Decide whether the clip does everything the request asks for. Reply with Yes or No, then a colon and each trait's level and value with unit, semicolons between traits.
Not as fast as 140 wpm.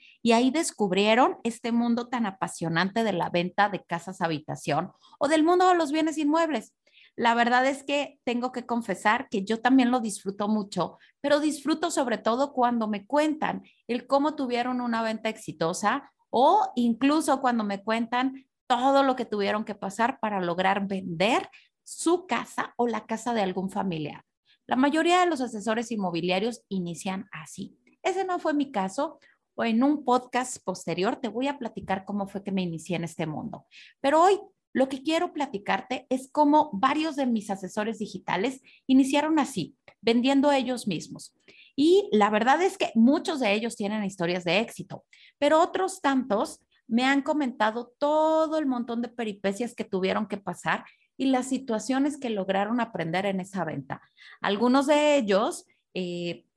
No: average, 165 wpm